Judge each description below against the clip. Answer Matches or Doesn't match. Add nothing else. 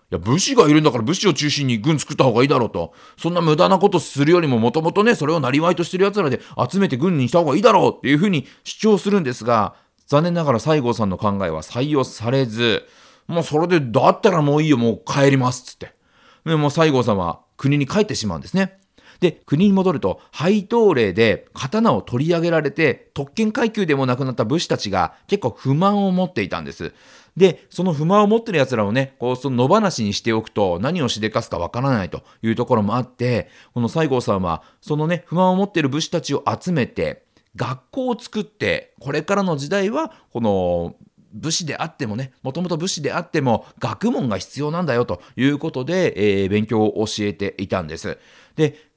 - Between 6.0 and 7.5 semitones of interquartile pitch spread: Matches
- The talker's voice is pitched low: Doesn't match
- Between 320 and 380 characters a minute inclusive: Doesn't match